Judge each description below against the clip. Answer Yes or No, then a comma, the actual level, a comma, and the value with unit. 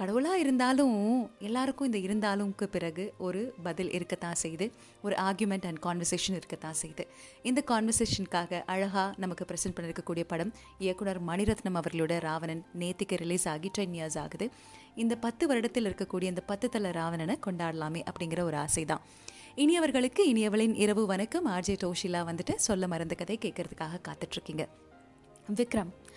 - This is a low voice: No, high, 190 Hz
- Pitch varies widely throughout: No, average, 4.1 semitones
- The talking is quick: Yes, fast, 135 wpm